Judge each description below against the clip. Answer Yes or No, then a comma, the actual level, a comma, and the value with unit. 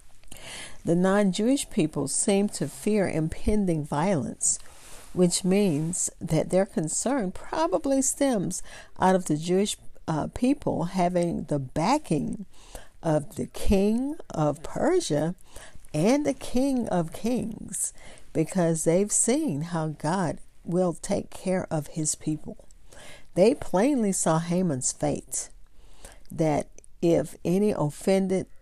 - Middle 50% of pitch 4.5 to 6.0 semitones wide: Yes, average, 4.9 semitones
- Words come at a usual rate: No, slow, 115 wpm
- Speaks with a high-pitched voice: No, medium, 180 Hz